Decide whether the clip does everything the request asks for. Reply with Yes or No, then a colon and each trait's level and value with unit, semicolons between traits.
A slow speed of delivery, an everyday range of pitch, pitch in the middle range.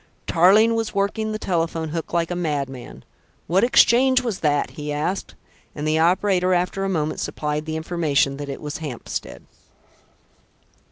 No: average, 155 wpm; average, 4.5 semitones; medium, 165 Hz